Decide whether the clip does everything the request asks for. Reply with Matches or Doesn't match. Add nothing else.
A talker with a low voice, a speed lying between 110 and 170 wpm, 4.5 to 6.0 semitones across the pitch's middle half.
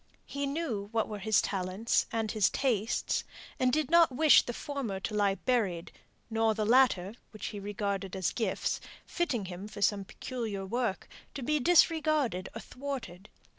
Doesn't match